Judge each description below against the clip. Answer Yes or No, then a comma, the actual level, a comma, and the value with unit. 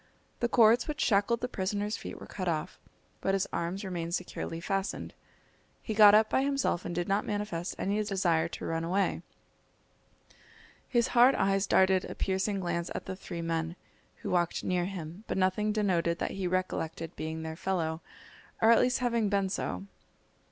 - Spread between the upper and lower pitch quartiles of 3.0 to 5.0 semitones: Yes, average, 3.6 semitones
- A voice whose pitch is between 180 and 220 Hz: Yes, high, 190 Hz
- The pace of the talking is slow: No, average, 175 wpm